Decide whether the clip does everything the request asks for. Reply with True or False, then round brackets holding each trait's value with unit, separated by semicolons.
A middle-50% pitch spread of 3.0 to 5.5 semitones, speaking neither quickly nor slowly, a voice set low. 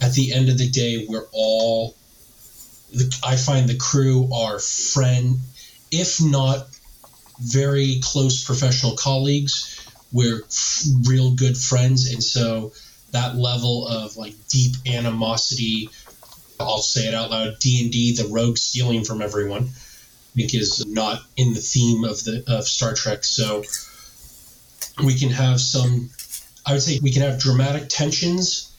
False (2.4 semitones; 150 wpm; 125 Hz)